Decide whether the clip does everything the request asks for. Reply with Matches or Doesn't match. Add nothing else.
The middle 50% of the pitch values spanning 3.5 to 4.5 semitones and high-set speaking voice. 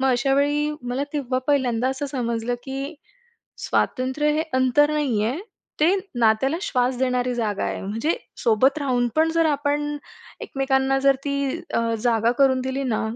Doesn't match